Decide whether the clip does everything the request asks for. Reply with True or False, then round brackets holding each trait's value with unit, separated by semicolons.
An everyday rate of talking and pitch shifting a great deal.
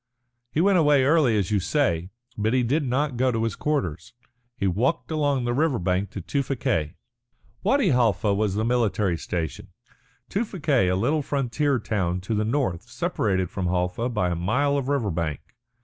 True (175 wpm; 7.0 semitones)